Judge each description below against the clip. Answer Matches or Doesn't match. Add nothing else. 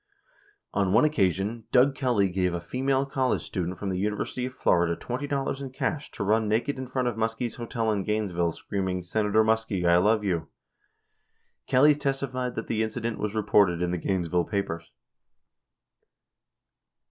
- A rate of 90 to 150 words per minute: Doesn't match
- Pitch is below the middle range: Matches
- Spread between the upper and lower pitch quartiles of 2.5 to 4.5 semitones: Doesn't match